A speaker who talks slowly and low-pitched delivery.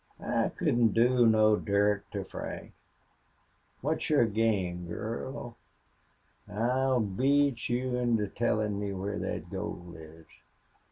Yes: slow, 115 wpm; low, 110 Hz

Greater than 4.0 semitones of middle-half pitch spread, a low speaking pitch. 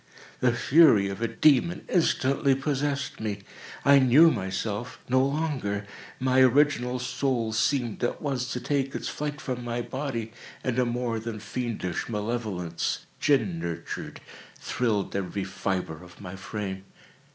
Yes: average, 4.8 semitones; low, 120 Hz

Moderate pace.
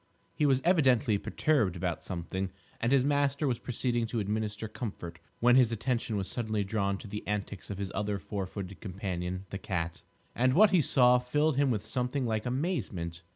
Yes: average, 185 wpm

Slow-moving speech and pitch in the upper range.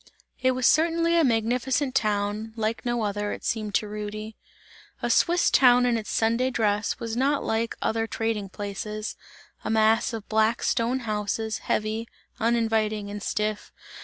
No: average, 155 wpm; high, 225 Hz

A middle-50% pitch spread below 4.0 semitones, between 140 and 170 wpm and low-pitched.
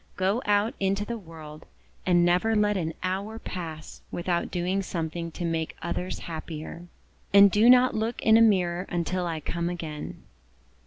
No: average, 3.5 semitones; average, 160 wpm; medium, 180 Hz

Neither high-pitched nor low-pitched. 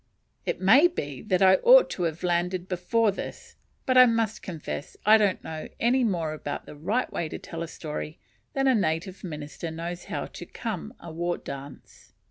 Yes: medium, 180 Hz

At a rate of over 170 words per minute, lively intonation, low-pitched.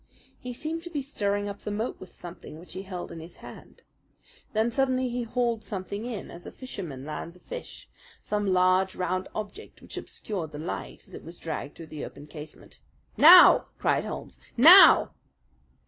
No: average, 180 wpm; wide, 6.0 semitones; high, 200 Hz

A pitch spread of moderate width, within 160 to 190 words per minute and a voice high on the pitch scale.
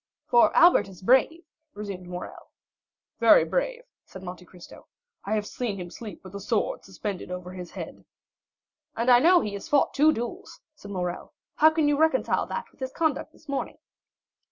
No: wide, 8.0 semitones; average, 180 wpm; high, 215 Hz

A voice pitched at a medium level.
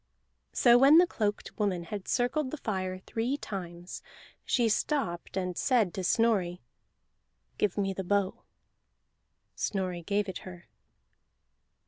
No: high, 200 Hz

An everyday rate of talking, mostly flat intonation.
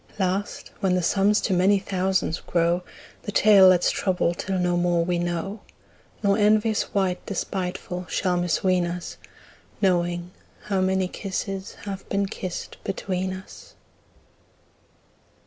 No: slow, 130 wpm; narrow, 1.8 semitones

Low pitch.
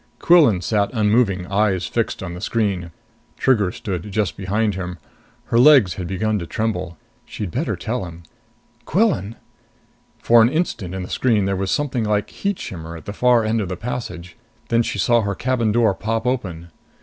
Yes: low, 105 Hz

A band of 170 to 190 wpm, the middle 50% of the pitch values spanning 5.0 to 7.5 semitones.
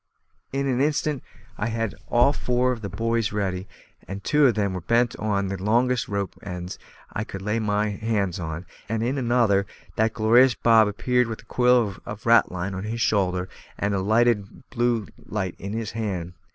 No: average, 185 wpm; average, 3.2 semitones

